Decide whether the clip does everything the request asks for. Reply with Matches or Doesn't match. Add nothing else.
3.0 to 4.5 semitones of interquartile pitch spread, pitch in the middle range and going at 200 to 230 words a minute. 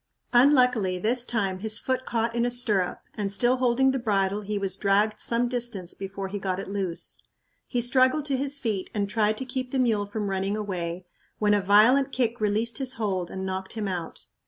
Doesn't match